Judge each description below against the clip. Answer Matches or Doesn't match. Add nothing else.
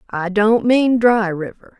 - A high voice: Matches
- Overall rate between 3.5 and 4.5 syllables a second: Matches